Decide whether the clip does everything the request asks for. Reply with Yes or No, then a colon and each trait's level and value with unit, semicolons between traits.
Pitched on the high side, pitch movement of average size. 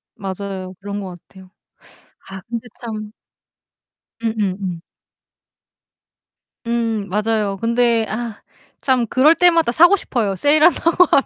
Yes: high, 225 Hz; average, 3.8 semitones